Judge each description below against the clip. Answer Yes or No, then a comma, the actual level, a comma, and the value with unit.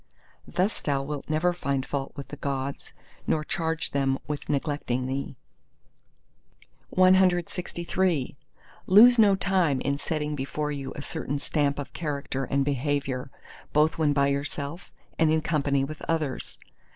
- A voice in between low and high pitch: Yes, medium, 145 Hz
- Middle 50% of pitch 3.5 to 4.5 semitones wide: No, average, 2.8 semitones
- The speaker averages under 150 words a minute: Yes, average, 140 wpm